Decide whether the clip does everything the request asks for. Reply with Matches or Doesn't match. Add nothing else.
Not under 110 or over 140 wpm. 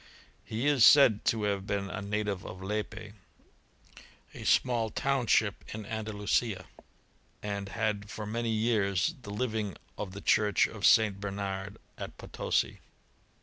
Matches